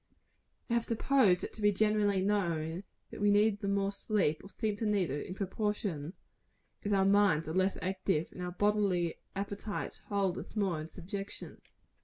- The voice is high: Yes, high, 200 Hz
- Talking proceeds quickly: No, average, 180 wpm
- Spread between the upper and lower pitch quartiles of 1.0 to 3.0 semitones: Yes, narrow, 2.4 semitones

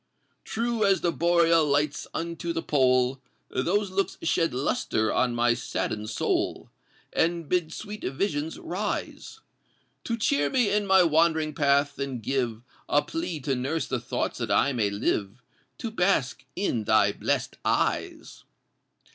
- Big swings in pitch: Yes, wide, 5.9 semitones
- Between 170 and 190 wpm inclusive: No, average, 145 wpm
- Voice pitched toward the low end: No, medium, 155 Hz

